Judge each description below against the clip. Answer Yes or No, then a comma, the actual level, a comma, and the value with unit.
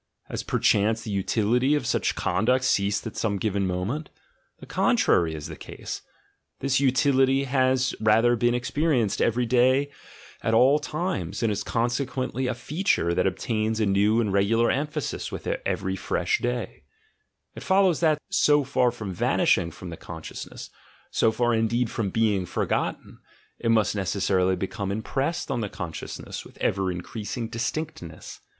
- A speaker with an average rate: Yes, average, 155 wpm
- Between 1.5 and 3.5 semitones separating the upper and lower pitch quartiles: No, average, 4.8 semitones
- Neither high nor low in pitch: No, low, 115 Hz